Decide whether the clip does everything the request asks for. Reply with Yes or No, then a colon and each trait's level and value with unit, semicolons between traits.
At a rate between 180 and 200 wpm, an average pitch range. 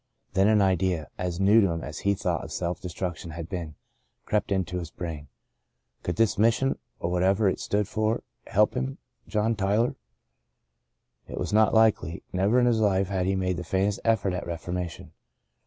Yes: average, 185 wpm; average, 3.1 semitones